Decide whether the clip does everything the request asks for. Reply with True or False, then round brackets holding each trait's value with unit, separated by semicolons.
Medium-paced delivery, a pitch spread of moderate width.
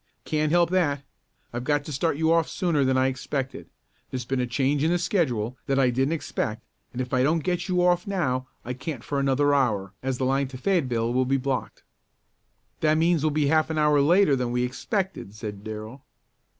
False (210 wpm; 4.0 semitones)